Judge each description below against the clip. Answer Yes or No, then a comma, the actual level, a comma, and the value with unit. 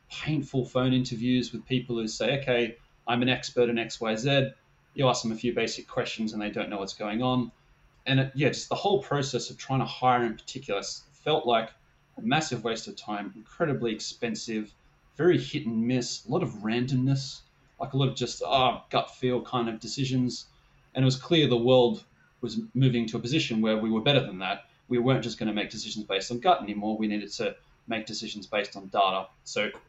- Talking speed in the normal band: No, fast, 210 wpm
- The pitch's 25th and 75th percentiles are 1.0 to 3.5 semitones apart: Yes, average, 2.9 semitones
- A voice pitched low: Yes, low, 120 Hz